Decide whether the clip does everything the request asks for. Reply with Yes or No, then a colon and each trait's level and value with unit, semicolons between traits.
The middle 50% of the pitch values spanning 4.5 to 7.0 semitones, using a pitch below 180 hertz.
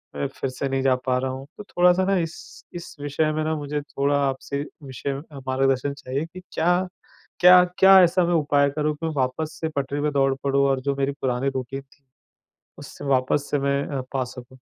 No: narrow, 2.6 semitones; medium, 140 Hz